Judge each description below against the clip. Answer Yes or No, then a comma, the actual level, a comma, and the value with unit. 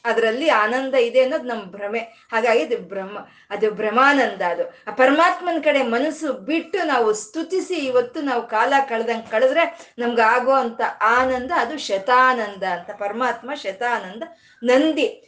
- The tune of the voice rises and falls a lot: No, average, 5.0 semitones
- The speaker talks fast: Yes, fast, 125 wpm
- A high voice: Yes, very high, 250 Hz